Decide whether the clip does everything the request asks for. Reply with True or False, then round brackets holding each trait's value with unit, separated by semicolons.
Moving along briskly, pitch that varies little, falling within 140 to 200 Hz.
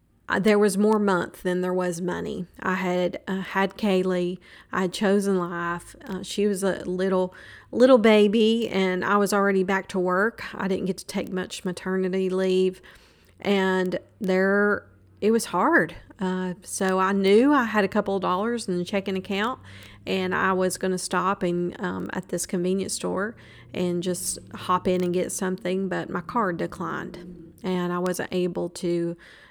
False (175 wpm; 1.7 semitones; 185 Hz)